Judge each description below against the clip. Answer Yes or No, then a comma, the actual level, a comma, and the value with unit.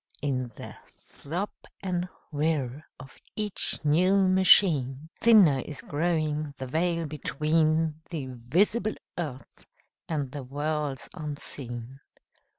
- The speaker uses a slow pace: Yes, slow, 105 wpm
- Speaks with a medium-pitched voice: Yes, medium, 155 Hz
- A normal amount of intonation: Yes, average, 4.1 semitones